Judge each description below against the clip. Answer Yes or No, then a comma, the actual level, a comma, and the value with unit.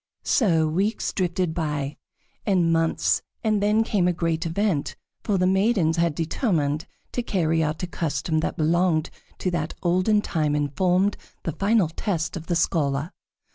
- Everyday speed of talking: Yes, average, 160 wpm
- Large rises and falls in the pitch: No, average, 3.3 semitones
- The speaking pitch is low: No, medium, 170 Hz